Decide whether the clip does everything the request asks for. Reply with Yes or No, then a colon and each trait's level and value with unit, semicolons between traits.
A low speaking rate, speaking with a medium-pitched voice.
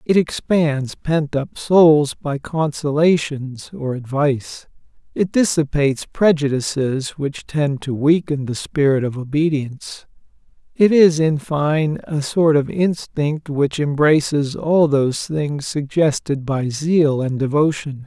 Yes: slow, 125 wpm; medium, 150 Hz